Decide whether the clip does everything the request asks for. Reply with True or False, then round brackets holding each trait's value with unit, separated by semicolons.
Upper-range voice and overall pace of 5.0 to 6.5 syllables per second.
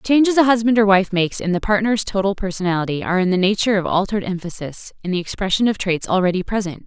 False (195 Hz; 7.0 syllables/s)